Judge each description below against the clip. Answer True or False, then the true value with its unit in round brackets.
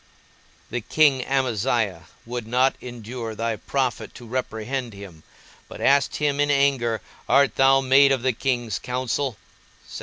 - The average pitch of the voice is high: False (125 Hz)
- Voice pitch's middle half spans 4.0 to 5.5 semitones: False (2.9 semitones)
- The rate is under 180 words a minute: True (140 wpm)